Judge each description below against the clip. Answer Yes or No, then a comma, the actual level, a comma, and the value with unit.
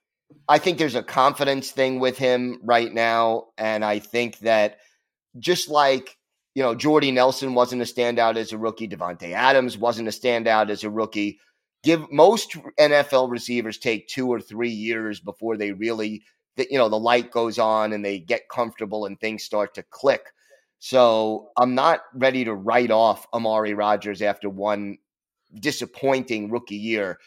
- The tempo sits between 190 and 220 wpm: No, average, 165 wpm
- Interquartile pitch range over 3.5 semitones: No, average, 3.0 semitones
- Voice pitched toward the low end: Yes, low, 115 Hz